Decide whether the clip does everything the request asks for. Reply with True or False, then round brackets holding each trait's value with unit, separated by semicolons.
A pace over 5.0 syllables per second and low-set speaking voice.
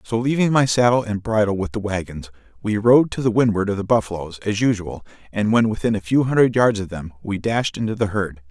True (5.7 syllables/s; 110 Hz)